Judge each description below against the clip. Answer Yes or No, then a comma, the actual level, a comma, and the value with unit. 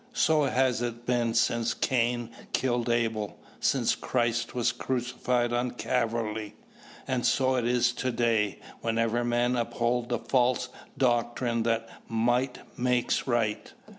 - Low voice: Yes, low, 120 Hz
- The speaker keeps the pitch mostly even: Yes, narrow, 1.2 semitones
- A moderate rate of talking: No, slow, 130 wpm